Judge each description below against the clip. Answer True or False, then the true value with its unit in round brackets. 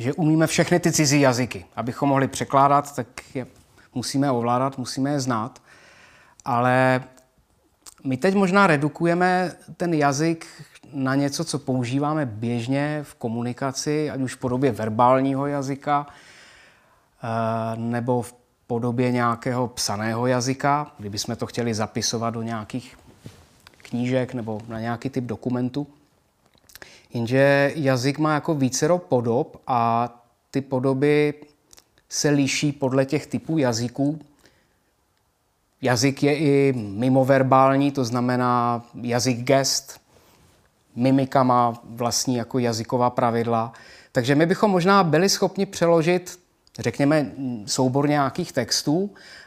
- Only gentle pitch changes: False (3.2 semitones)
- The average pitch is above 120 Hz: True (130 Hz)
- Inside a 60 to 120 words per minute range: True (115 wpm)